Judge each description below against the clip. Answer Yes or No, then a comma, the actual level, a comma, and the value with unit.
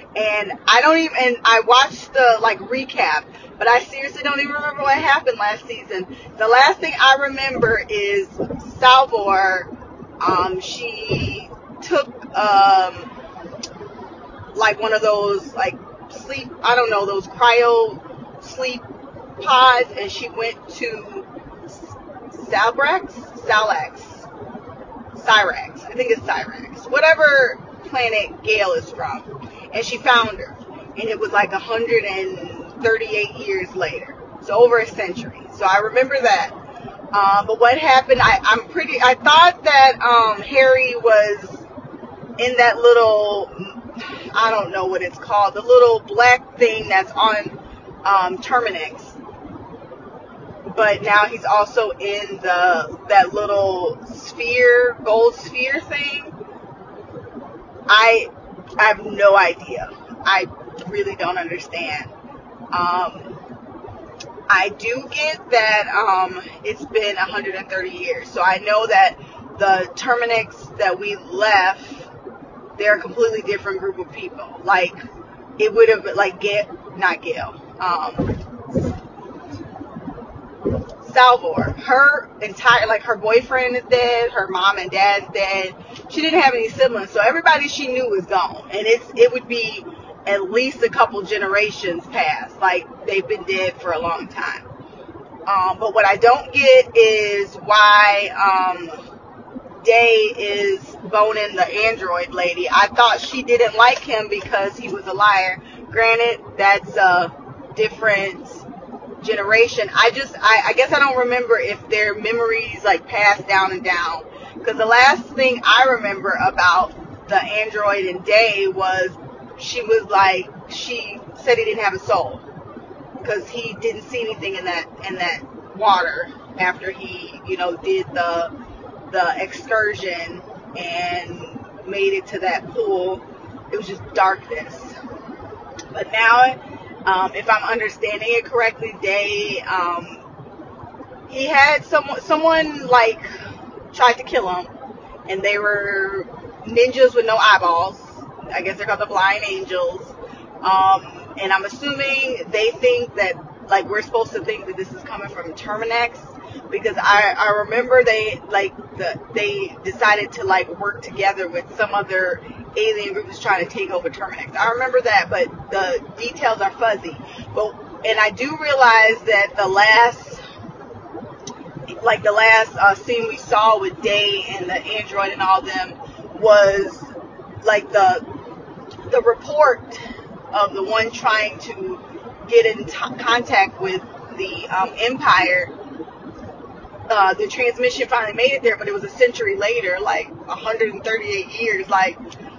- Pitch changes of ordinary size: No, wide, 6.6 semitones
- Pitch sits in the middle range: No, high, 230 Hz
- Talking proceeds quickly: No, average, 140 wpm